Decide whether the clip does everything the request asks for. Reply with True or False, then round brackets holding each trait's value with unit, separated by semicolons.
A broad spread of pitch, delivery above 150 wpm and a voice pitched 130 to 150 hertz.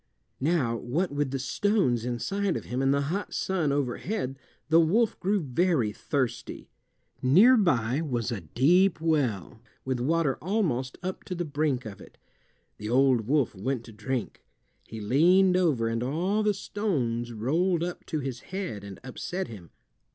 True (6.7 semitones; 160 wpm; 140 Hz)